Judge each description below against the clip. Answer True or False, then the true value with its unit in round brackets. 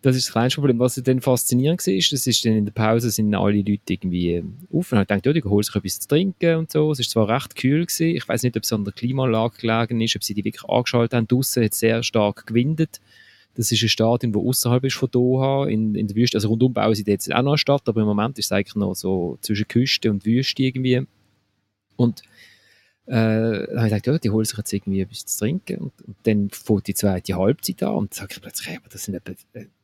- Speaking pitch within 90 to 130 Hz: True (115 Hz)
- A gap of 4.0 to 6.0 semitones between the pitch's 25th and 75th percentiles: False (3.5 semitones)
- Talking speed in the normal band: False (260 wpm)